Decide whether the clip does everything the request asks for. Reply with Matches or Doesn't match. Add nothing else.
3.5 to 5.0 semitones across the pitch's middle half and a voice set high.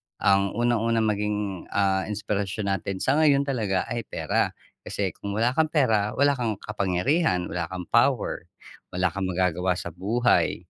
Doesn't match